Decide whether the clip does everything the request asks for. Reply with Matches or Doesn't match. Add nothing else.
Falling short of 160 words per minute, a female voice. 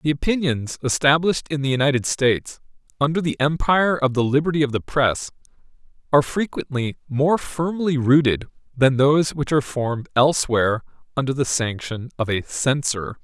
Doesn't match